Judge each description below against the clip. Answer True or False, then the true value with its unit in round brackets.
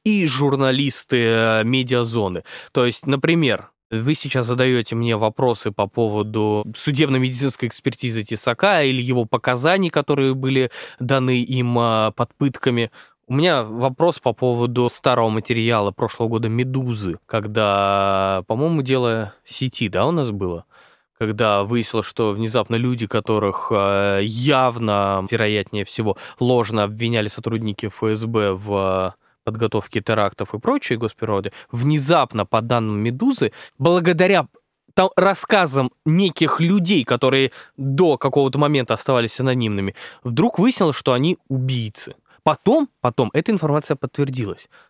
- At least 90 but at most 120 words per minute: True (115 wpm)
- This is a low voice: True (120 Hz)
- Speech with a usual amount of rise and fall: True (4.1 semitones)